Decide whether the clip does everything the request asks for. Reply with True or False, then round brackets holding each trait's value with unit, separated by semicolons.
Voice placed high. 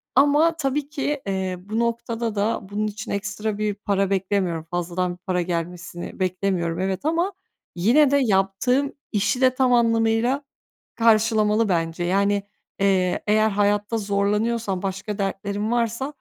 True (205 Hz)